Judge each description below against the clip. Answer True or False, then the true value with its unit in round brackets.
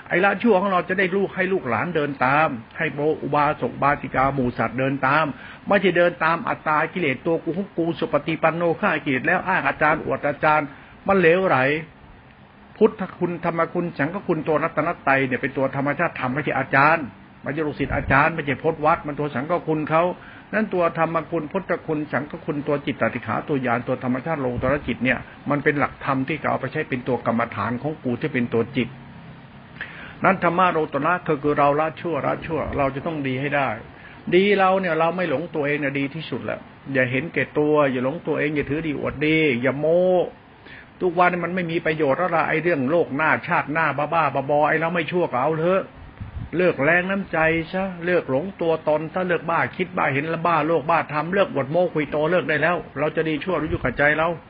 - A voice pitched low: False (155 Hz)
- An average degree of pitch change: True (3.6 semitones)